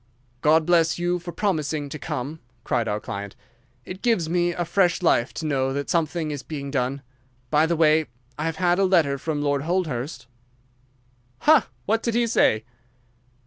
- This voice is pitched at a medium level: Yes, medium, 160 Hz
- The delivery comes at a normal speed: Yes, average, 170 wpm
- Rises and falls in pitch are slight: No, average, 3.8 semitones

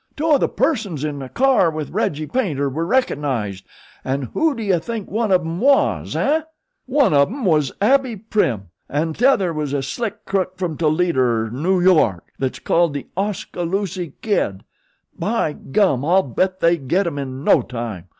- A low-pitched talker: No, medium, 170 Hz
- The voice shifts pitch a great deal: Yes, wide, 6.8 semitones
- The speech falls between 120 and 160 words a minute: No, average, 180 wpm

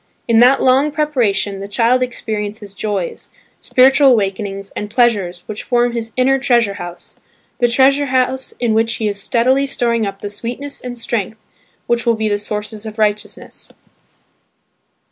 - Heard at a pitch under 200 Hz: No, high, 230 Hz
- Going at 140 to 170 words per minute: Yes, average, 150 wpm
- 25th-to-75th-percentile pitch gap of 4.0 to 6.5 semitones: No, average, 3.5 semitones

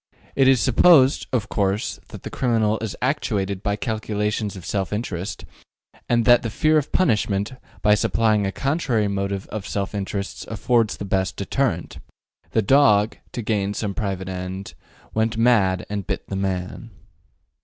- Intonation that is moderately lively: Yes, average, 3.1 semitones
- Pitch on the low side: Yes, low, 105 Hz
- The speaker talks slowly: No, average, 160 wpm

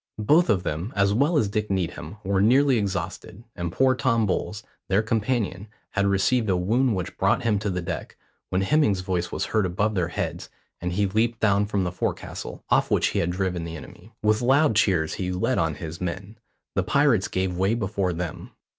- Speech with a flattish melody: No, average, 3.4 semitones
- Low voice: Yes, low, 100 Hz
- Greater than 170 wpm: Yes, average, 200 wpm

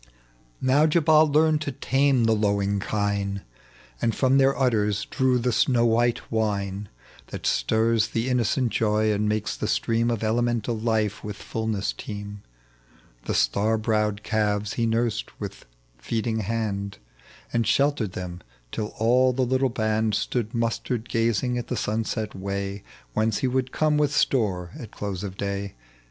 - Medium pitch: No, low, 110 Hz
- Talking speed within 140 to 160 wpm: Yes, average, 155 wpm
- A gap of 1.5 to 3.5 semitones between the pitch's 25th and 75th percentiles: Yes, average, 3.2 semitones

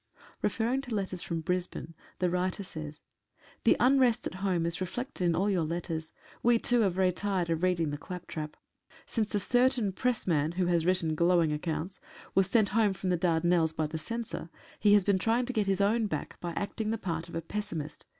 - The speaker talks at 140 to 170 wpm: No, fast, 205 wpm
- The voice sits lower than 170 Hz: No, medium, 185 Hz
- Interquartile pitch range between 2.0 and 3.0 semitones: No, average, 4.0 semitones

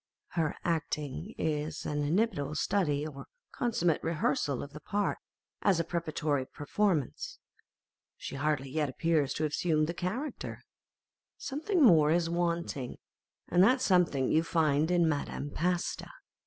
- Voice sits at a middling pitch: Yes, medium, 160 Hz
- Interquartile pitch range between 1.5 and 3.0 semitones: No, average, 3.4 semitones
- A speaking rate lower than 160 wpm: Yes, average, 140 wpm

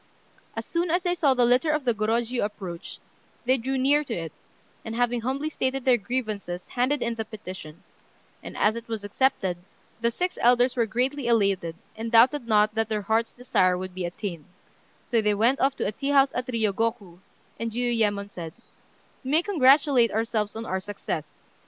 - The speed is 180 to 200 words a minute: Yes, average, 185 wpm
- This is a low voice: No, high, 230 Hz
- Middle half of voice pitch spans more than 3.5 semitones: Yes, average, 3.9 semitones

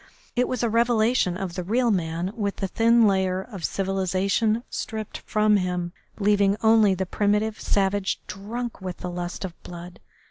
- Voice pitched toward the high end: Yes, high, 200 Hz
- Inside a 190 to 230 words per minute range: No, average, 165 wpm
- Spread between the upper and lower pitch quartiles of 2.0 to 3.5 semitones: Yes, average, 3.0 semitones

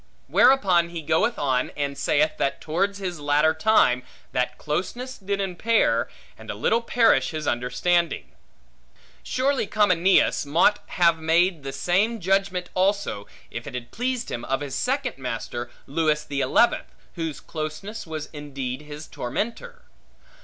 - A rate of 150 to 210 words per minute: No, average, 140 wpm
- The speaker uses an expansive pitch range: Yes, wide, 5.7 semitones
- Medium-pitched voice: Yes, medium, 165 Hz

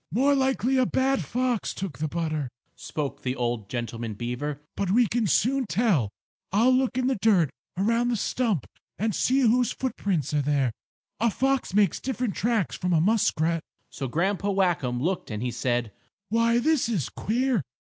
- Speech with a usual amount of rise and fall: No, wide, 8.6 semitones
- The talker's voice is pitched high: Yes, high, 200 Hz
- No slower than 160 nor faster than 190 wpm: Yes, average, 170 wpm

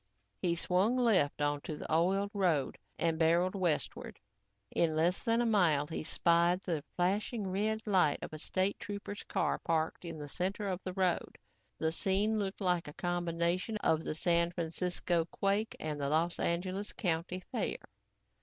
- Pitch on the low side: No, medium, 175 Hz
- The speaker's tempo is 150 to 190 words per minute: Yes, average, 165 wpm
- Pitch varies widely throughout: No, average, 3.2 semitones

